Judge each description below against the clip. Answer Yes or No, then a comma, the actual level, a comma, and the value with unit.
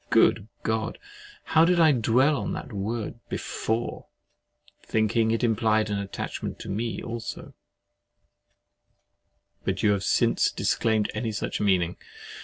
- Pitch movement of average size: No, narrow, 2.2 semitones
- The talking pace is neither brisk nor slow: No, slow, 125 wpm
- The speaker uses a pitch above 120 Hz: No, low, 110 Hz